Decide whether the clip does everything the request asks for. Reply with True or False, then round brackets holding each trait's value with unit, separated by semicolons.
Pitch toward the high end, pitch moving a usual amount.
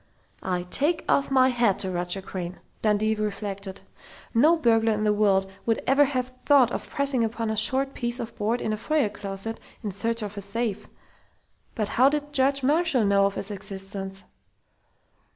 True (220 Hz; 4.5 semitones)